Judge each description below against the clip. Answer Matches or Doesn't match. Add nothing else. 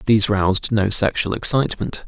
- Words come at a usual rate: Matches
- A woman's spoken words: Doesn't match